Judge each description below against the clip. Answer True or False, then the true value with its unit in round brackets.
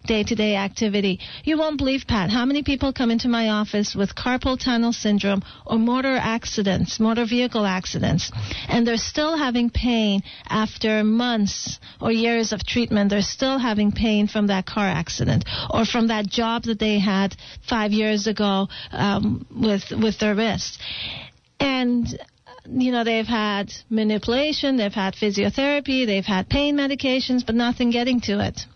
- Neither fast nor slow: True (160 wpm)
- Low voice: False (225 Hz)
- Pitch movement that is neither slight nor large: True (3.0 semitones)